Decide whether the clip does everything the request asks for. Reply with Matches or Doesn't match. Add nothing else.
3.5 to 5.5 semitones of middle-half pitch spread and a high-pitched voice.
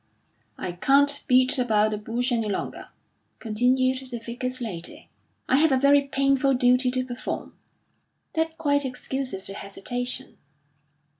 Doesn't match